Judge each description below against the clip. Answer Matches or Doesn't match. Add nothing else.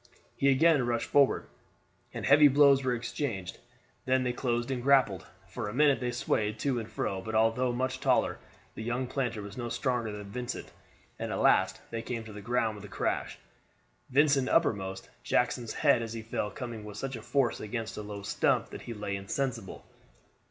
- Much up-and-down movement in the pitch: Doesn't match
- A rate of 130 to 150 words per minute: Doesn't match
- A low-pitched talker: Matches